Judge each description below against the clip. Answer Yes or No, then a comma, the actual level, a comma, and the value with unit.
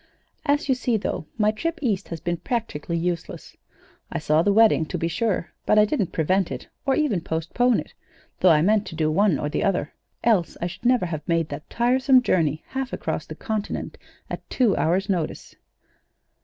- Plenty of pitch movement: Yes, wide, 6.0 semitones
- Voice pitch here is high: Yes, high, 195 Hz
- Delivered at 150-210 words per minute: Yes, average, 195 wpm